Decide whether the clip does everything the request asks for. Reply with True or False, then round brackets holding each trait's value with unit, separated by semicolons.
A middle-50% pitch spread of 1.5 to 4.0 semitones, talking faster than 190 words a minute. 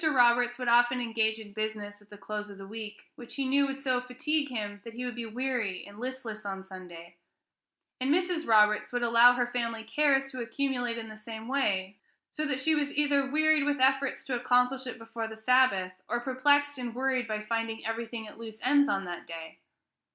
True (3.5 semitones; 205 wpm)